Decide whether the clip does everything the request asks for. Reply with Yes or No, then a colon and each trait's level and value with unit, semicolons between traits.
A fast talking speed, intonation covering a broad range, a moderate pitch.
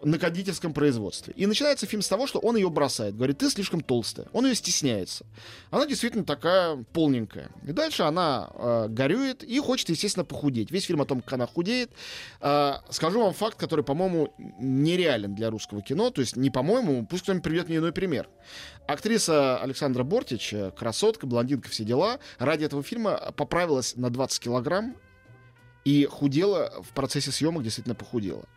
Yes: fast, 170 wpm; wide, 7.5 semitones; medium, 145 Hz